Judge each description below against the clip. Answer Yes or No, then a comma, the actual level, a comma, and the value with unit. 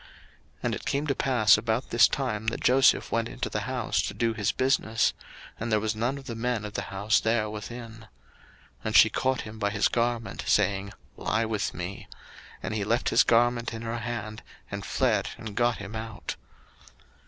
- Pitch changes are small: Yes, narrow, 1.8 semitones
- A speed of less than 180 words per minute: No, average, 200 wpm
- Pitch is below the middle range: Yes, low, 115 Hz